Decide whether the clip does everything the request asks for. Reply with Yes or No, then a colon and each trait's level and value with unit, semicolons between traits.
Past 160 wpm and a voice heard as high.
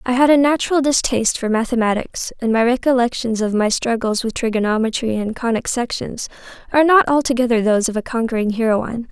Yes: average, 170 wpm; high, 240 Hz